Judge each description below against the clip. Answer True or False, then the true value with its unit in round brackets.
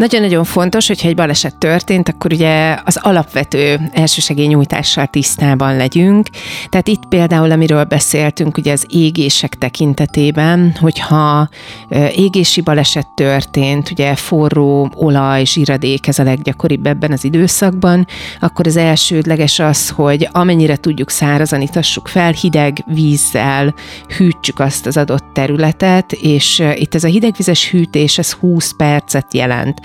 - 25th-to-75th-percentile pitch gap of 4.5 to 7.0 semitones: False (2.9 semitones)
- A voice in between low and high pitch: True (155 Hz)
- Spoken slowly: False (130 wpm)